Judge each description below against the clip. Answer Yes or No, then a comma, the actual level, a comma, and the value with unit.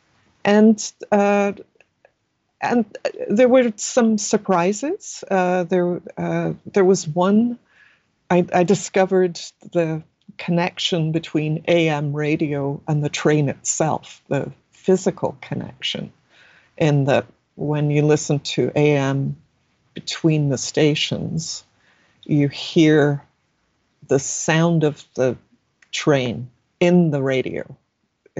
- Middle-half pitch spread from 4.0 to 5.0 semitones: Yes, average, 4.5 semitones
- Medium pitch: Yes, medium, 160 Hz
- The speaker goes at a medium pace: No, slow, 100 wpm